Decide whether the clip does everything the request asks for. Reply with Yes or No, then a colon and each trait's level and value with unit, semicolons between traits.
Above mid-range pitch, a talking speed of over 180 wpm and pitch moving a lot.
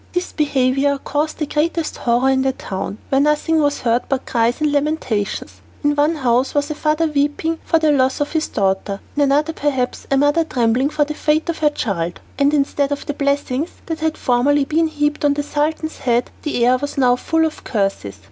No: very high, 285 Hz; fast, 205 wpm; average, 3.1 semitones